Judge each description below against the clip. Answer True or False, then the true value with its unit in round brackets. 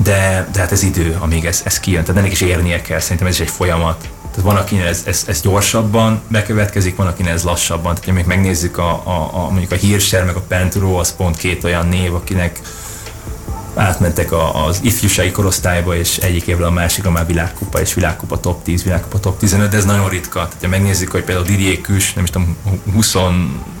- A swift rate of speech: True (210 wpm)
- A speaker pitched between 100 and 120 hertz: False (90 Hz)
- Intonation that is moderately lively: False (2.3 semitones)